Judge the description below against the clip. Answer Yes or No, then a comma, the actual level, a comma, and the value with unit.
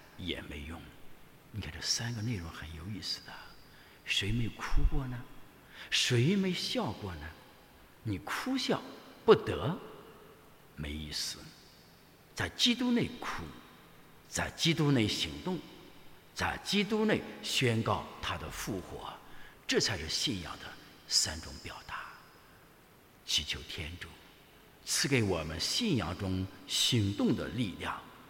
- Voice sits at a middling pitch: No, low, 110 Hz